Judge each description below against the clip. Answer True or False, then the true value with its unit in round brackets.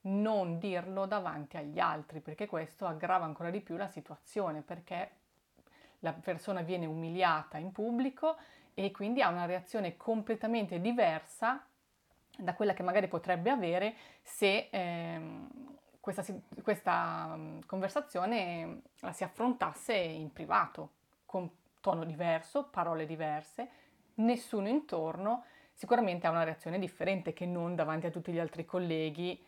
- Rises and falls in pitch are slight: False (4.4 semitones)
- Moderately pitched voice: True (180 Hz)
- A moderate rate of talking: True (130 wpm)